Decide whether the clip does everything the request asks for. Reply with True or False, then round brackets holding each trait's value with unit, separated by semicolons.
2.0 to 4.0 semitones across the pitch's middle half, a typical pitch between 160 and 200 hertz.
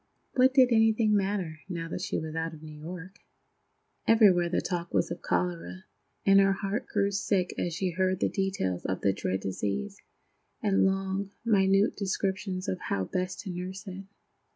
True (2.7 semitones; 190 Hz)